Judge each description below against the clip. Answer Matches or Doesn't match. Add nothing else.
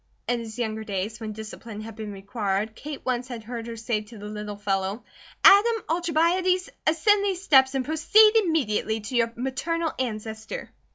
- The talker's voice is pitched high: Matches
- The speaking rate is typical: Matches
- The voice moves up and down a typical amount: Doesn't match